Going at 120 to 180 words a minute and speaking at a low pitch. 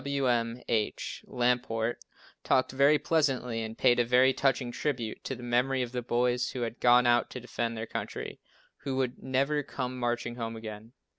Yes: average, 175 wpm; low, 125 Hz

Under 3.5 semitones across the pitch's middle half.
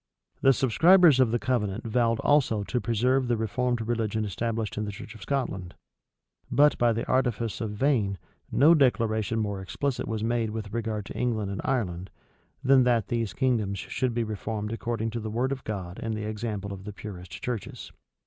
Yes: average, 2.9 semitones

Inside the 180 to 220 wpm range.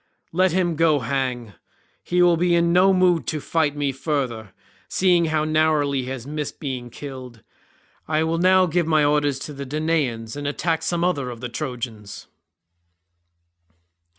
No: average, 160 wpm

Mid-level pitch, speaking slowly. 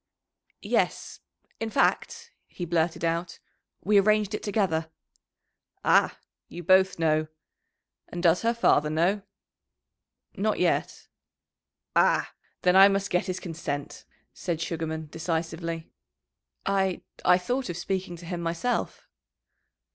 Yes: medium, 175 Hz; slow, 115 wpm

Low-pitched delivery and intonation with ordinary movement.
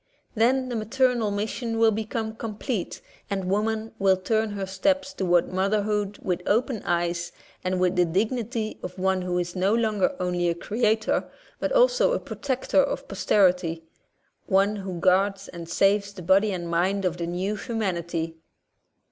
No: high, 200 Hz; average, 3.5 semitones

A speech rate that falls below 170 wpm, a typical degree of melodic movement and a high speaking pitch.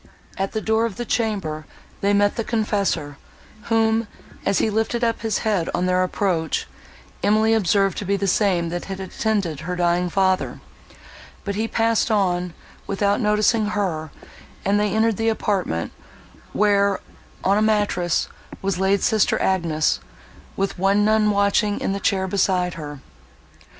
Yes: average, 155 wpm; average, 3.0 semitones; high, 200 Hz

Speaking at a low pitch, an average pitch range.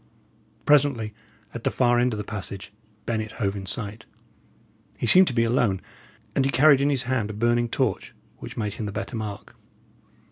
Yes: low, 115 Hz; average, 3.6 semitones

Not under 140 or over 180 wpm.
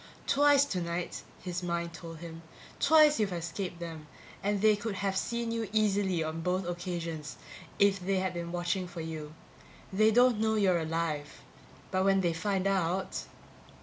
Yes: average, 160 wpm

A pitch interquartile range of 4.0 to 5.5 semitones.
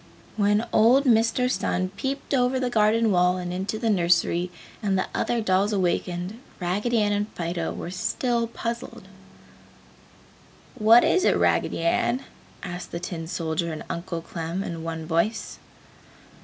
Yes: average, 4.7 semitones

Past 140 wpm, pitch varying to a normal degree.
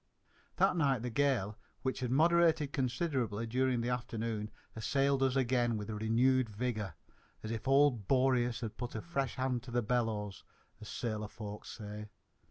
Yes: average, 160 wpm; average, 3.2 semitones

